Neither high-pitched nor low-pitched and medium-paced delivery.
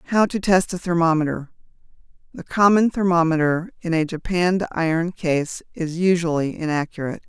No: medium, 170 Hz; slow, 125 wpm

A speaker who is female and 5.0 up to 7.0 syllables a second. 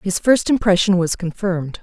Yes: female; 5.2 syllables/s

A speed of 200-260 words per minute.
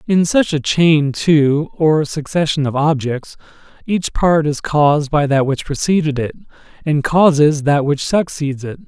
No: average, 160 wpm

